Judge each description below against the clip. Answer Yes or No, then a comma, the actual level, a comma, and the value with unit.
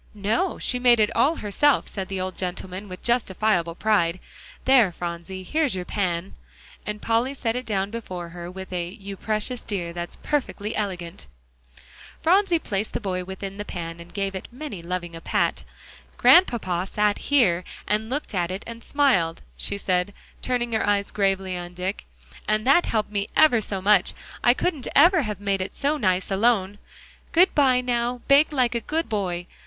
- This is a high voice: Yes, high, 205 Hz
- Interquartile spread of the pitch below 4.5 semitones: No, average, 4.8 semitones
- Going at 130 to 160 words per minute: No, average, 175 wpm